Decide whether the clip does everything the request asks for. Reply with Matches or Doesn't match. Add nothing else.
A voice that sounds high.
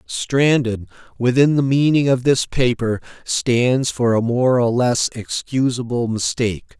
Doesn't match